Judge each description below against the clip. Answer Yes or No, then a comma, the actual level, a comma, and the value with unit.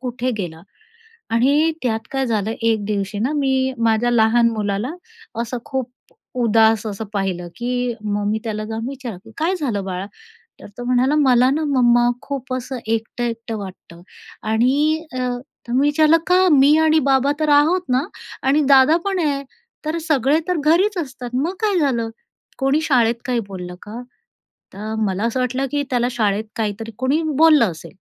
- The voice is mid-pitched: No, high, 245 Hz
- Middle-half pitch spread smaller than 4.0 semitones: No, average, 4.3 semitones